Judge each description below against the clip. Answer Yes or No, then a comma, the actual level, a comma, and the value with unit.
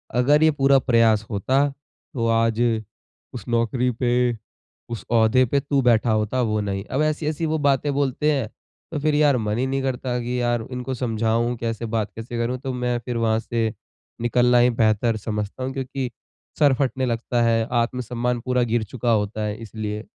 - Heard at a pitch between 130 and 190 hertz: No, low, 120 Hz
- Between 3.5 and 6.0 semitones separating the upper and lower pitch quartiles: No, narrow, 2.5 semitones